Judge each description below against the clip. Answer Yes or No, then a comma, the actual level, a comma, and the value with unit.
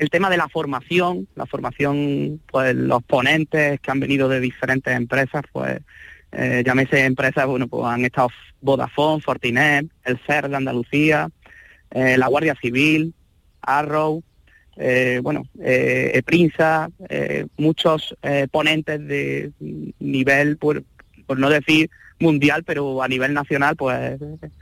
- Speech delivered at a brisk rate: No, average, 135 wpm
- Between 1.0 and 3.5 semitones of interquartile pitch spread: Yes, average, 3.2 semitones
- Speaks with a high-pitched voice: No, medium, 140 Hz